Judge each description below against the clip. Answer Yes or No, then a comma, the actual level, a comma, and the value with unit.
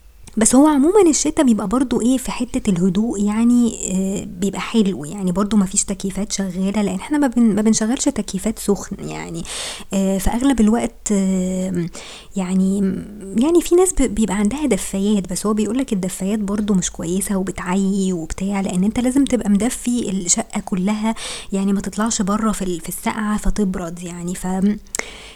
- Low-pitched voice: No, high, 205 Hz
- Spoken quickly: Yes, fast, 145 wpm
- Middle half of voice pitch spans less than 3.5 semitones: Yes, average, 2.9 semitones